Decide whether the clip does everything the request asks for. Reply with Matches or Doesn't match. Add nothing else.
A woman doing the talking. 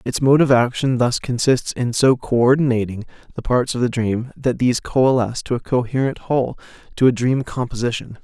Doesn't match